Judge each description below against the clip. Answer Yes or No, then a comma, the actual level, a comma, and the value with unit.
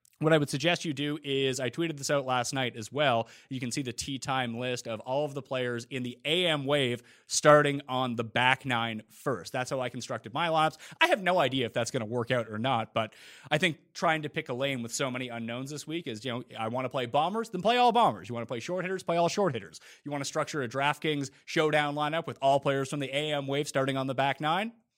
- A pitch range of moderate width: Yes, average, 3.7 semitones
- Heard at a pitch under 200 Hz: Yes, low, 135 Hz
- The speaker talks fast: Yes, fast, 265 wpm